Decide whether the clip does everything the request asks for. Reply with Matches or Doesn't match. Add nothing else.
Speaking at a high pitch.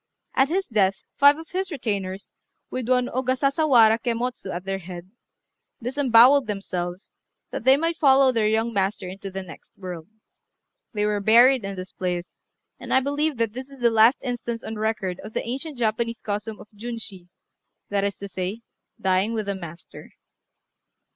Matches